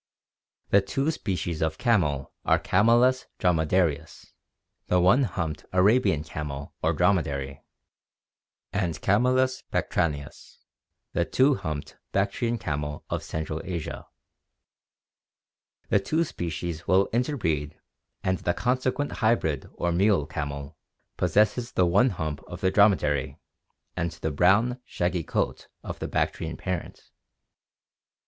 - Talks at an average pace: No, slow, 115 wpm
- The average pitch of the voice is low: Yes, very low, 90 Hz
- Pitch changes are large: Yes, wide, 6.0 semitones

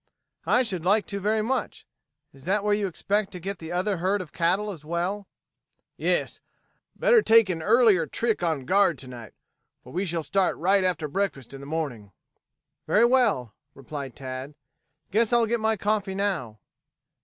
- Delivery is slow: No, average, 175 wpm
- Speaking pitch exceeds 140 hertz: Yes, medium, 185 Hz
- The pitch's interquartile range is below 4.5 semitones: No, average, 5.2 semitones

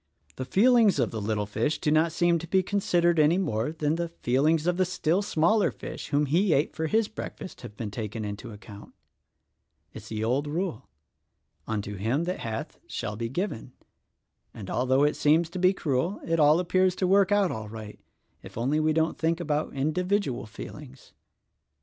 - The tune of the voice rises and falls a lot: Yes, wide, 7.0 semitones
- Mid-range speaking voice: Yes, medium, 155 Hz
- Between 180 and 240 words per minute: Yes, average, 185 wpm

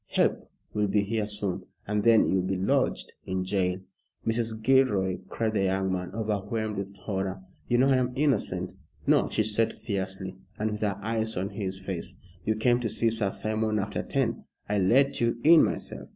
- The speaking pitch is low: Yes, low, 105 Hz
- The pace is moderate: Yes, average, 185 wpm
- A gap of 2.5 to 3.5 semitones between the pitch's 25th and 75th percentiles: Yes, average, 2.8 semitones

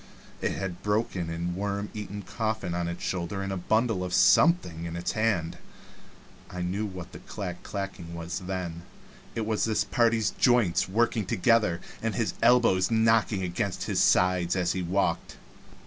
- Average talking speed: Yes, average, 165 wpm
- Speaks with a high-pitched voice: No, very low, 95 Hz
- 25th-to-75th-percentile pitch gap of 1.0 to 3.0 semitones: No, average, 3.8 semitones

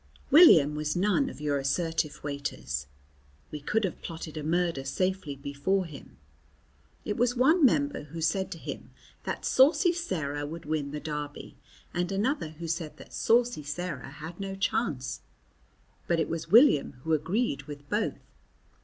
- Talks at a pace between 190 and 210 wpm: No, average, 155 wpm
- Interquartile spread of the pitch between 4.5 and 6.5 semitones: Yes, average, 5.1 semitones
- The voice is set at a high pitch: No, medium, 165 Hz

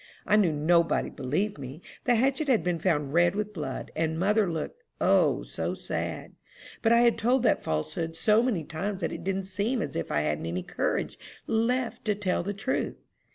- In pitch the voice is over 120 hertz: Yes, high, 190 Hz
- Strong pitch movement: Yes, wide, 6.0 semitones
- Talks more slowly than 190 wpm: No, average, 195 wpm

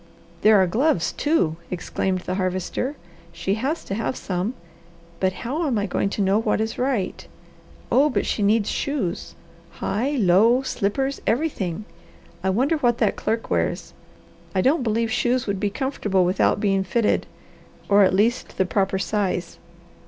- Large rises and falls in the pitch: No, average, 4.8 semitones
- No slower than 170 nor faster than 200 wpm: No, average, 160 wpm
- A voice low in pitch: No, high, 210 Hz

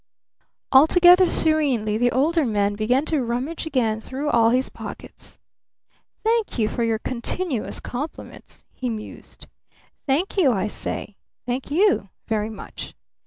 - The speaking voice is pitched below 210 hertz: No, very high, 255 Hz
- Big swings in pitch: Yes, wide, 5.9 semitones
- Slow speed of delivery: Yes, slow, 130 wpm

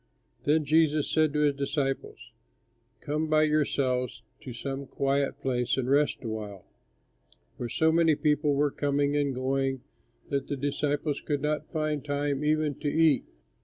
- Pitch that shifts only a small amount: Yes, narrow, 2.0 semitones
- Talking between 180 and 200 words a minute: No, average, 155 wpm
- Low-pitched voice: No, medium, 145 Hz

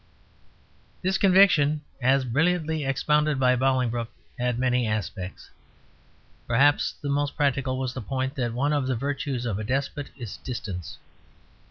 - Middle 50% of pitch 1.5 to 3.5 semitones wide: Yes, average, 3.1 semitones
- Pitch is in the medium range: No, low, 130 Hz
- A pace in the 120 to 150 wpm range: Yes, average, 140 wpm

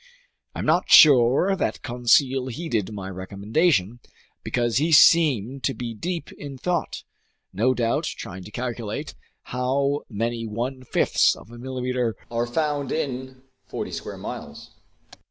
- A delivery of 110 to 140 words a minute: Yes, slow, 135 wpm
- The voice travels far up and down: No, average, 3.3 semitones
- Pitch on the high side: No, low, 125 Hz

